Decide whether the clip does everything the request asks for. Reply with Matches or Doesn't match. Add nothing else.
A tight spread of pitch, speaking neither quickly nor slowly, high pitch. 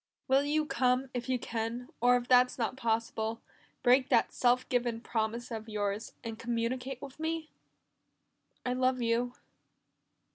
Matches